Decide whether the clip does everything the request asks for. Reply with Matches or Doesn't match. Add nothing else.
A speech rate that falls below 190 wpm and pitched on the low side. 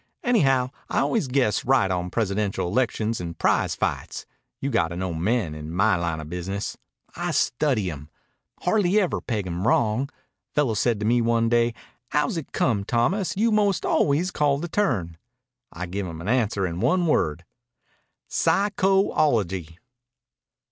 Matches